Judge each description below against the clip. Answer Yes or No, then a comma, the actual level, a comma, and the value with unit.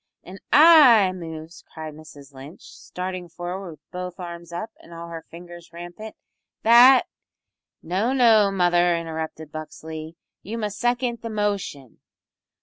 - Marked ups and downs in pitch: No, average, 4.6 semitones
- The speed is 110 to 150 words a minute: Yes, average, 140 wpm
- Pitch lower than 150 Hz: No, medium, 175 Hz